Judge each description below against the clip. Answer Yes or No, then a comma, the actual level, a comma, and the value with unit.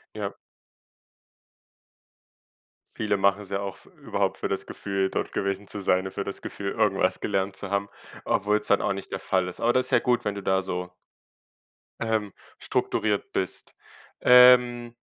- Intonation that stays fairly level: Yes, narrow, 1.7 semitones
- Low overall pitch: Yes, low, 100 Hz